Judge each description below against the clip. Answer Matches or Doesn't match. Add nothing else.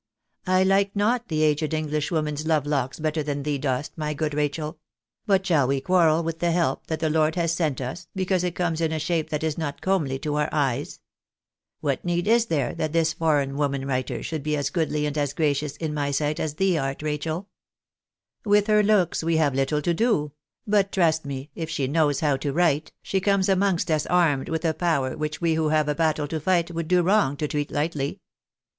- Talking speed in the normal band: Doesn't match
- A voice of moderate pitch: Matches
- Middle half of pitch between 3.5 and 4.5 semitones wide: Doesn't match